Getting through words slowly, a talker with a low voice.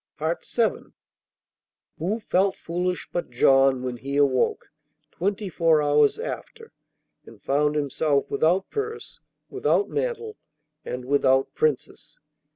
No: slow, 110 wpm; medium, 160 Hz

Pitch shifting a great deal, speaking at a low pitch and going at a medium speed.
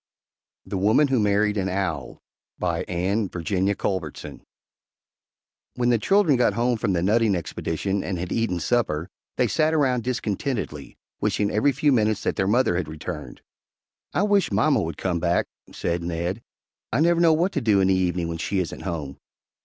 Yes: wide, 5.7 semitones; low, 100 Hz; average, 175 wpm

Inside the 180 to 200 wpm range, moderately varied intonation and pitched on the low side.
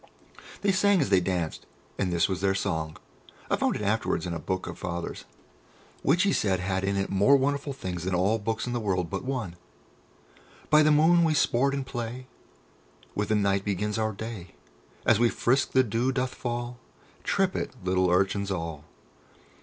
No: average, 185 wpm; wide, 5.7 semitones; low, 105 Hz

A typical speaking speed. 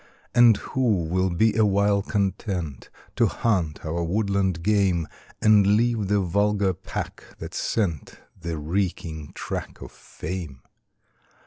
No: slow, 120 wpm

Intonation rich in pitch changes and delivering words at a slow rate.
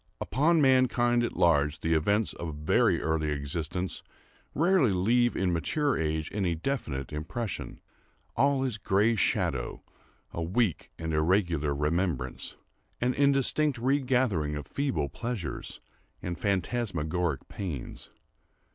Yes: wide, 7.8 semitones; slow, 110 wpm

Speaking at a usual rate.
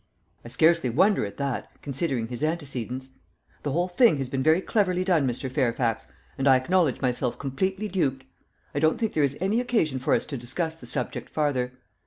Yes: average, 190 wpm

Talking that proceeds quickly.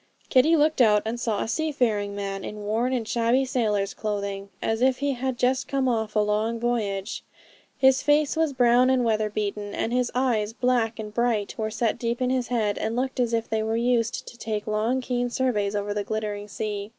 Yes: fast, 210 wpm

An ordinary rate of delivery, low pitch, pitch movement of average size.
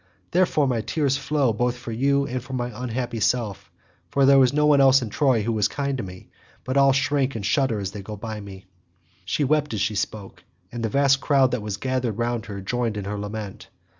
No: fast, 225 wpm; low, 125 Hz; average, 4.3 semitones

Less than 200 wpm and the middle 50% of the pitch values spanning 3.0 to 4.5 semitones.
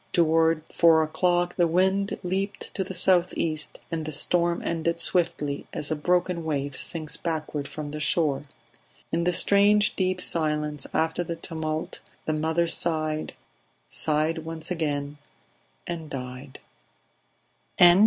No: slow, 135 wpm; narrow, 2.4 semitones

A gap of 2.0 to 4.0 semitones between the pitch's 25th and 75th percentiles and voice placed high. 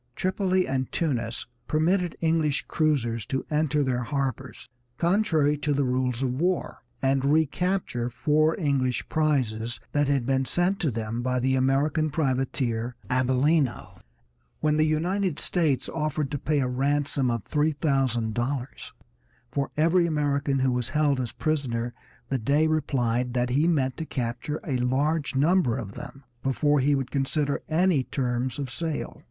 No: average, 3.4 semitones; medium, 140 Hz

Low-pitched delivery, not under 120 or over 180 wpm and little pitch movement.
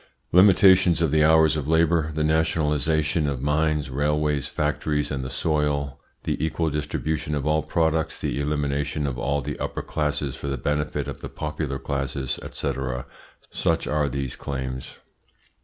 Yes: very low, 75 Hz; average, 155 wpm; narrow, 1.8 semitones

